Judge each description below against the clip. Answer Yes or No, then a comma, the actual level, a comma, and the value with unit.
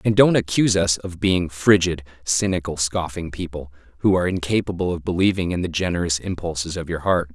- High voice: No, very low, 85 Hz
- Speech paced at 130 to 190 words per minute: Yes, average, 180 wpm